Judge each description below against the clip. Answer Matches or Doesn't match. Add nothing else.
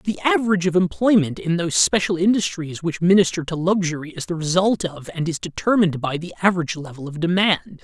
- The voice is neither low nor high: Matches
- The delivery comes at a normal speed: Matches